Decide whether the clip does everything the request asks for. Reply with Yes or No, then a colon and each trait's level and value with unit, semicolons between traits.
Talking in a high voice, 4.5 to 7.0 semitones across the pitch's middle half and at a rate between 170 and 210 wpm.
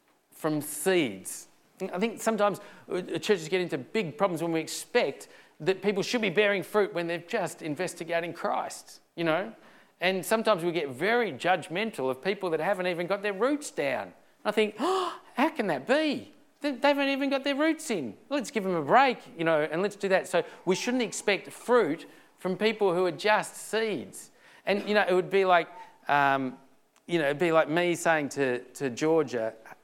Yes: high, 195 Hz; average, 4.8 semitones; average, 190 wpm